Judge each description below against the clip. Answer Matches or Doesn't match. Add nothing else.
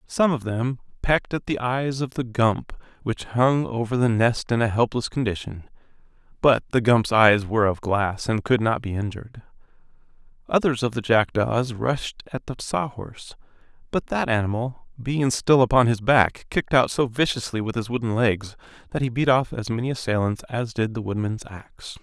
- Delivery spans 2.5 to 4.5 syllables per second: Doesn't match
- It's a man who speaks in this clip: Matches